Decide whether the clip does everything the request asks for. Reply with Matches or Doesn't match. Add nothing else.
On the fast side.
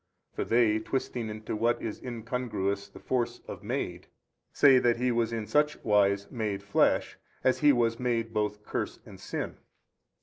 Doesn't match